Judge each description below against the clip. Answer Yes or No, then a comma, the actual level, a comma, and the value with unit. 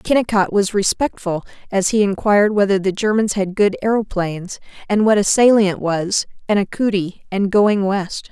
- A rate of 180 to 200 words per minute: No, average, 165 wpm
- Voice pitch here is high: Yes, high, 200 Hz